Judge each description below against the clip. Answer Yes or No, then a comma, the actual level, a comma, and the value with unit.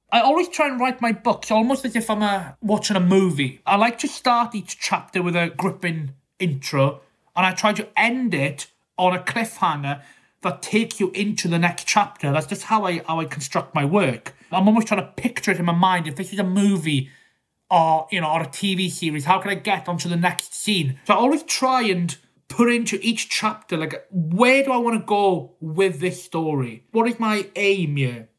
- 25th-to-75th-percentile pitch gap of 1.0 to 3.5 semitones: No, average, 4.9 semitones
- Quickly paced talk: Yes, fast, 220 wpm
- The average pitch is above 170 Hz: Yes, high, 190 Hz